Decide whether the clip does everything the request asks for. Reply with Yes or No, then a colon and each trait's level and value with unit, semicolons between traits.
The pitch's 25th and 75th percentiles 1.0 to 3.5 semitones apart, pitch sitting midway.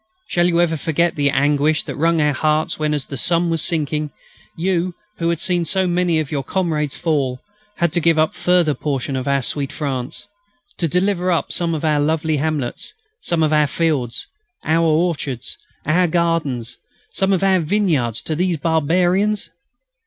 Yes: average, 2.9 semitones; medium, 160 Hz